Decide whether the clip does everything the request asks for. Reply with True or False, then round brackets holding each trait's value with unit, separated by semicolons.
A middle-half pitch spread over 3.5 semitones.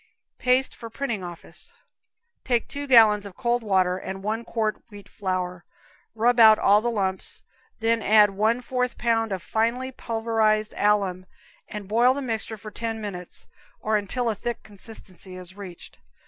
False (2.9 semitones)